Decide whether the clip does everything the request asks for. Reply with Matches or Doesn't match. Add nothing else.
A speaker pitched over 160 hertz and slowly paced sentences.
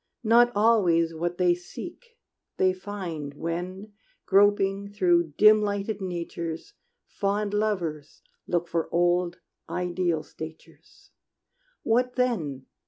Matches